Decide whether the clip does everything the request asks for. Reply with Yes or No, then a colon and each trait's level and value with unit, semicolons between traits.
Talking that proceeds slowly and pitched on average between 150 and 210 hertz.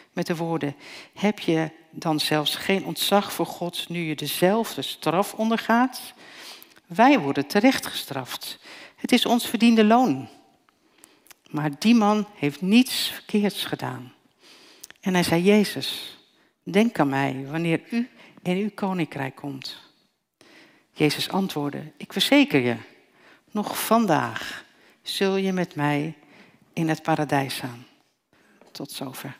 Yes: slow, 125 wpm; medium, 185 Hz